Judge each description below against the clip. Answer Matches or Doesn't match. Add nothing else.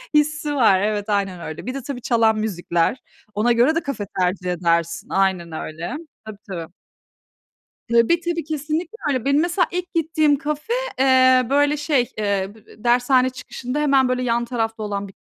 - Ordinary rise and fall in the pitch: Doesn't match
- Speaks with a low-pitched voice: Doesn't match